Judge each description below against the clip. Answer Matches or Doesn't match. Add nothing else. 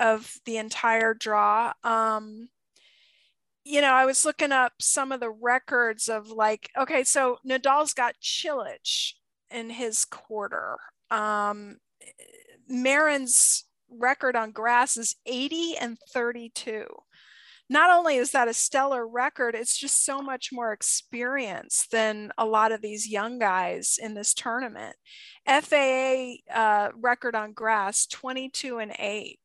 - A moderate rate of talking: Doesn't match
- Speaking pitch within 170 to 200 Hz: Doesn't match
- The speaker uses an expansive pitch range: Doesn't match